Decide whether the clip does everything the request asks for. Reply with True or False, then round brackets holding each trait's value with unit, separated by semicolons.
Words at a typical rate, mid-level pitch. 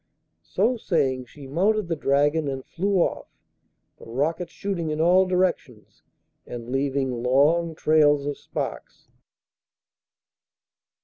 False (115 wpm; 150 Hz)